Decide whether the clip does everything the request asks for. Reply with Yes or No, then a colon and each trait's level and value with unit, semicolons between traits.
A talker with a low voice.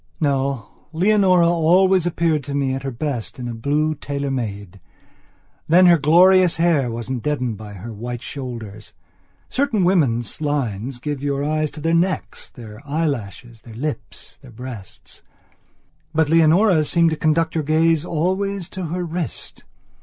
No: medium, 150 Hz